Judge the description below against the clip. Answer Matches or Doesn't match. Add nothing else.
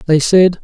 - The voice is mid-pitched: Matches